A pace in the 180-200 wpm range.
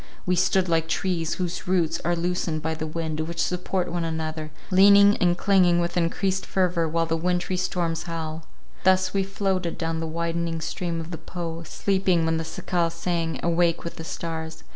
Yes: average, 185 wpm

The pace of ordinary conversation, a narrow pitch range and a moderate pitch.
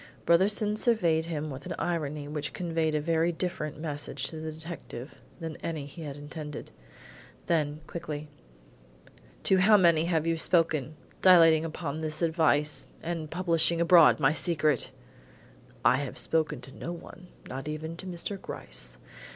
Yes: average, 150 wpm; narrow, 2.2 semitones; medium, 160 Hz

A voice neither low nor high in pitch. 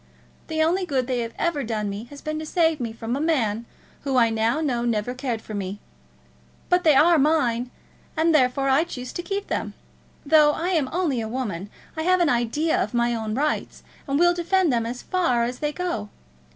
No: very high, 270 Hz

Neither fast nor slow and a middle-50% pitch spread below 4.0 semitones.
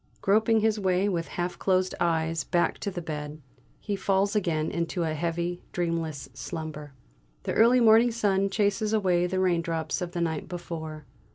Yes: average, 165 wpm; average, 3.4 semitones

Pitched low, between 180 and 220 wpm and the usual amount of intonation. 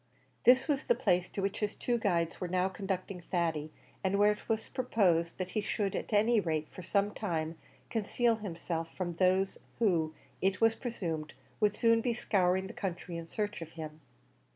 No: high, 190 Hz; average, 185 wpm; average, 3.9 semitones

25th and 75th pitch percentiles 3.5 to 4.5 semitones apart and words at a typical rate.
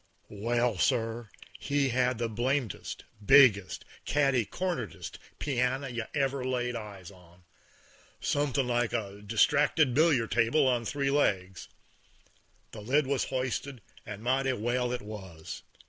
No: average, 3.9 semitones; slow, 125 wpm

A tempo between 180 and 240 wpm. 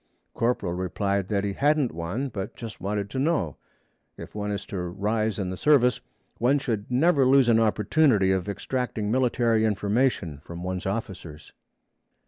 No: average, 155 wpm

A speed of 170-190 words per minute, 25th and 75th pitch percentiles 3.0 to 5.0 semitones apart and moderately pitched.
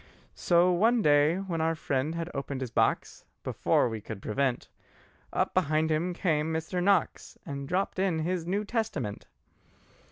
No: average, 155 wpm; average, 4.3 semitones; medium, 160 Hz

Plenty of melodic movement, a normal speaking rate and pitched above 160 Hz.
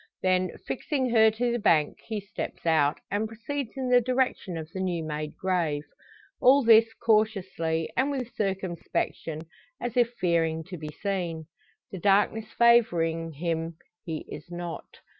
Yes: wide, 5.8 semitones; average, 150 wpm; high, 190 Hz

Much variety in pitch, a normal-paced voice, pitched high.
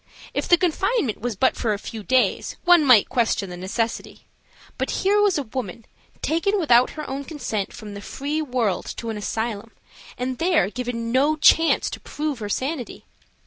Yes: wide, 5.7 semitones; average, 180 wpm; very high, 255 Hz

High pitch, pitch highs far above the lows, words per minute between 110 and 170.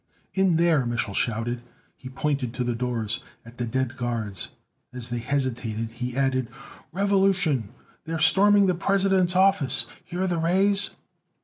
No: low, 135 Hz; wide, 7.3 semitones; average, 140 wpm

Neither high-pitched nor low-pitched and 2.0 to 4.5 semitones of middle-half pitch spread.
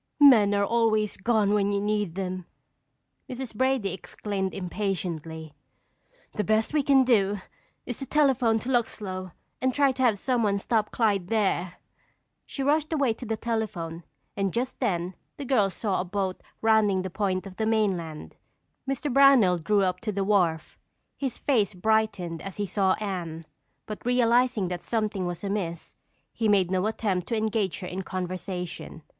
No: high, 205 Hz; average, 3.7 semitones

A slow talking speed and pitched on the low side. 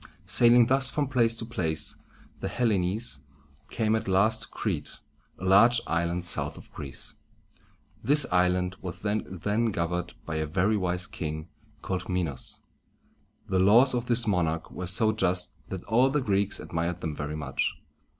No: average, 155 wpm; very low, 95 Hz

